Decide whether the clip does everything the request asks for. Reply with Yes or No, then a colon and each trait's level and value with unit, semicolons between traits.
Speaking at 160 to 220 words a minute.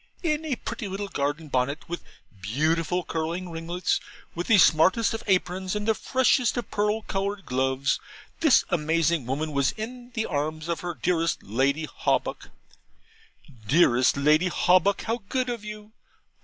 No: average, 150 wpm